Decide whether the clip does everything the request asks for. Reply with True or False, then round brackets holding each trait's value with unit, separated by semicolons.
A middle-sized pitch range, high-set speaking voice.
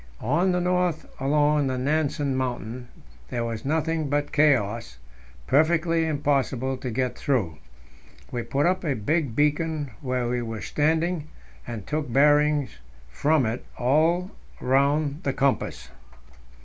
False (3.8 semitones; 145 Hz)